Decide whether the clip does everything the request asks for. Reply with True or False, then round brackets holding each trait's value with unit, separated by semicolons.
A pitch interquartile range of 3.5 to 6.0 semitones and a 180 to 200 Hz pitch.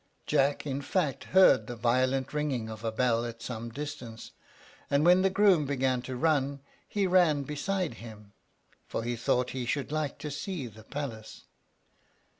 False (4.2 semitones; 135 Hz)